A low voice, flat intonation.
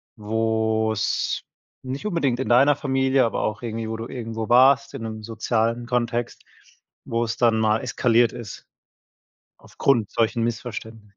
Yes: low, 115 Hz; narrow, 1.8 semitones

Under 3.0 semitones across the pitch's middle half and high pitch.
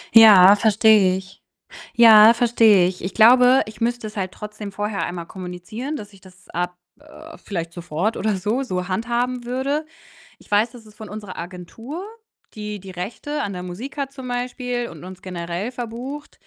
No: average, 4.7 semitones; high, 215 Hz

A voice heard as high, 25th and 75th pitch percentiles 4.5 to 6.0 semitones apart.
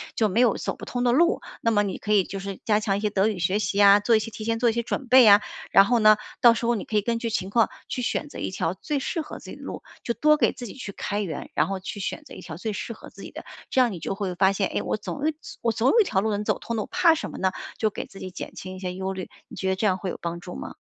No: high, 210 Hz; average, 3.4 semitones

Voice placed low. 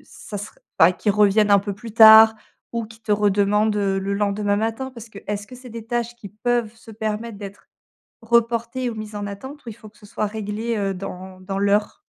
No: high, 215 Hz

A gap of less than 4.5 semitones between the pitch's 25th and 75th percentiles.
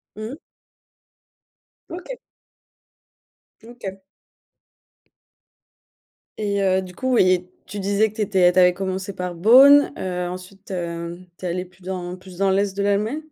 Yes: narrow, 2.5 semitones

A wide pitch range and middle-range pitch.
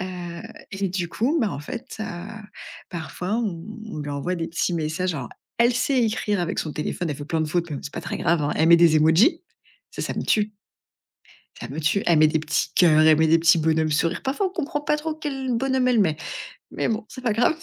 Yes: wide, 6.8 semitones; medium, 175 Hz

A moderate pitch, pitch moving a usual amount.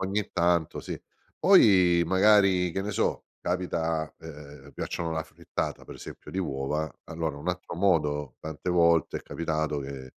No: very low, 85 Hz; average, 3.0 semitones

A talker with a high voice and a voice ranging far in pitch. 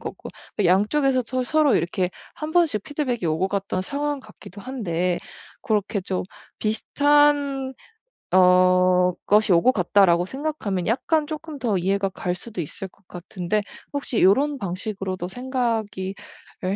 Yes: high, 205 Hz; wide, 6.6 semitones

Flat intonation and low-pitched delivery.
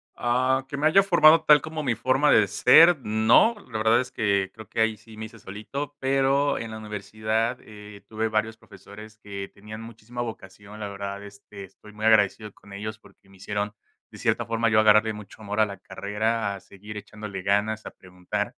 Yes: narrow, 2.2 semitones; low, 110 Hz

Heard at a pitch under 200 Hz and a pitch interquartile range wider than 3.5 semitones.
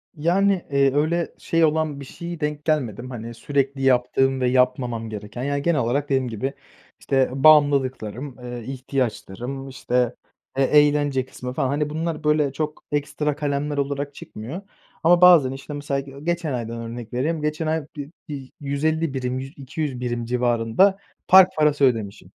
No: medium, 140 Hz; average, 3.2 semitones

